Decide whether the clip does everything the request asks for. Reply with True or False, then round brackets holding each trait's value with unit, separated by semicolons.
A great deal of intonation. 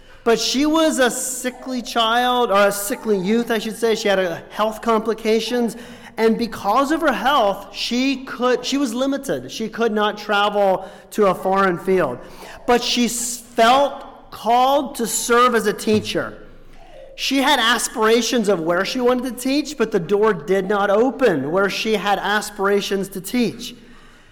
False (3.5 semitones)